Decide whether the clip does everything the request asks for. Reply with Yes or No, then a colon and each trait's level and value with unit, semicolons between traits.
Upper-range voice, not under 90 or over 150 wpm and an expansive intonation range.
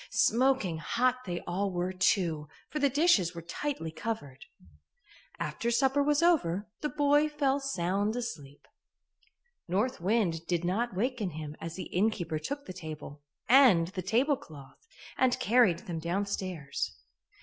Yes: high, 195 Hz; average, 140 wpm; wide, 7.2 semitones